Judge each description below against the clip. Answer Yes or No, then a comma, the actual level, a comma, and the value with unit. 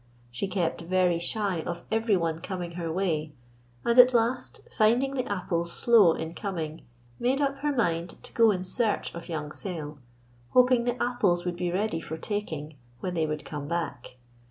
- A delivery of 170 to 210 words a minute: Yes, average, 175 wpm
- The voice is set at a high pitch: No, medium, 180 Hz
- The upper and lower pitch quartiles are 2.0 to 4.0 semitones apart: No, wide, 5.5 semitones